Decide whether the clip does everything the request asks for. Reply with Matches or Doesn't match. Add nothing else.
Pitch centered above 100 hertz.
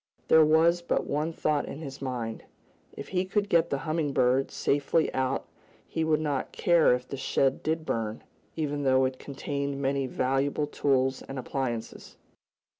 Matches